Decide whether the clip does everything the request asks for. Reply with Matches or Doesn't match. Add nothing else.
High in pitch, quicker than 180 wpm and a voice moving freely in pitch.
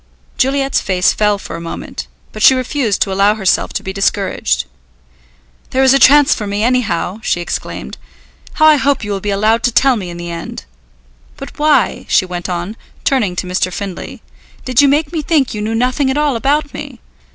Matches